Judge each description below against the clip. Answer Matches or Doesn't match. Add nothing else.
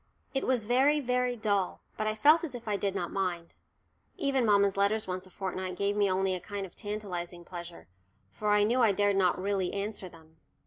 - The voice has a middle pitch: Doesn't match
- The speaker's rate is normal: Doesn't match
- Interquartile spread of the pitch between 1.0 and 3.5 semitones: Matches